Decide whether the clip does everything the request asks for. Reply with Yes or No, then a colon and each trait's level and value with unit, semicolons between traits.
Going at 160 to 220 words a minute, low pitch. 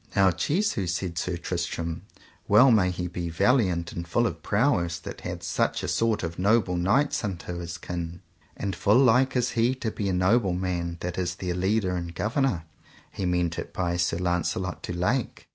Yes: average, 190 wpm; very low, 90 Hz